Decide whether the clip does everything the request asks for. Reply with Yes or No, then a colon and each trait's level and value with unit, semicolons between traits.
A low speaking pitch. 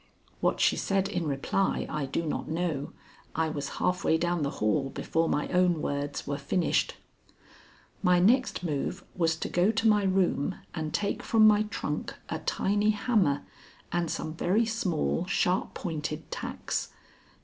No: medium, 175 Hz